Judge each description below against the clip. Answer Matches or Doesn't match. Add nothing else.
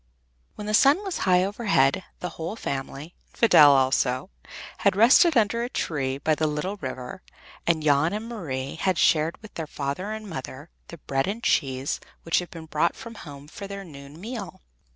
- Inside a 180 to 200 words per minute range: Matches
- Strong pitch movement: Matches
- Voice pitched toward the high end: Doesn't match